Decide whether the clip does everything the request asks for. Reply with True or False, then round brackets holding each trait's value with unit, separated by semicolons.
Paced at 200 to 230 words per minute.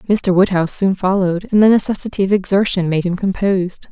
False (185 wpm)